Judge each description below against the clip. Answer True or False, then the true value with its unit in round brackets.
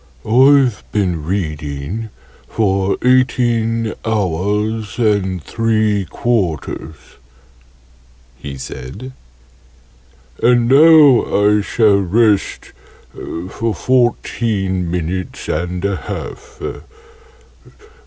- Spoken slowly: True (75 wpm)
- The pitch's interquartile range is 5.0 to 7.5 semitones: False (4.3 semitones)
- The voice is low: True (105 Hz)